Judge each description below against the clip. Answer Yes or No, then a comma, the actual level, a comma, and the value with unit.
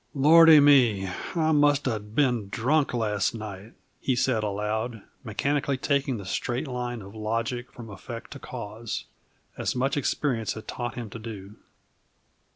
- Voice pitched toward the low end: Yes, low, 120 Hz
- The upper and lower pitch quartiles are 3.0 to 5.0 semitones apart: Yes, average, 4.1 semitones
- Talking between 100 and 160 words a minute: Yes, average, 150 wpm